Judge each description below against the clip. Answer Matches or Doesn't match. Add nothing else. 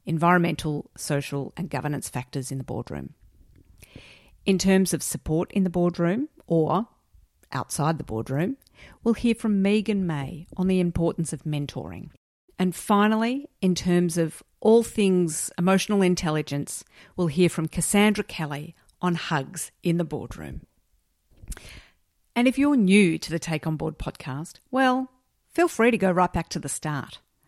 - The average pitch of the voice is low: Doesn't match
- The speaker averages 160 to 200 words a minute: Doesn't match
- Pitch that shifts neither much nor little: Matches